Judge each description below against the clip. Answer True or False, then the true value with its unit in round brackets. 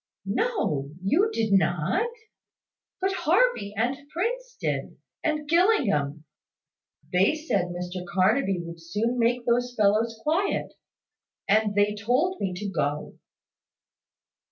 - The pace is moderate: False (110 wpm)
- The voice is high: True (220 Hz)